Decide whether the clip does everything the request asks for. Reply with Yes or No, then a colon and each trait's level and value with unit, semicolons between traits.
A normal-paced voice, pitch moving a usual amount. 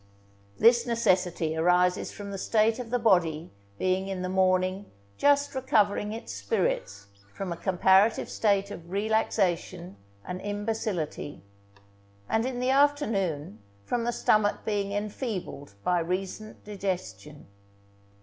No: slow, 120 wpm; average, 3.6 semitones